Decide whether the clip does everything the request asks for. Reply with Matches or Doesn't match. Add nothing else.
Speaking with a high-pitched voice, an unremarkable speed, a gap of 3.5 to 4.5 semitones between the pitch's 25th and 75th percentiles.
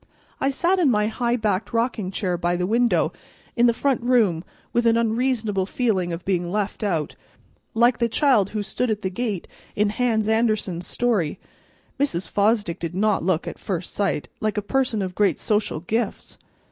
Matches